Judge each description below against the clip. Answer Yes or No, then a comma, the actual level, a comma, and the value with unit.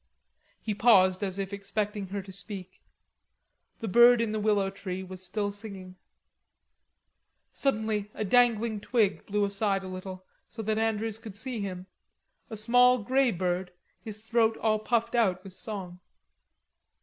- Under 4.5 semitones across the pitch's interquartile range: Yes, average, 2.8 semitones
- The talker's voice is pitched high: Yes, high, 210 Hz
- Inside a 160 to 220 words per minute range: No, average, 150 wpm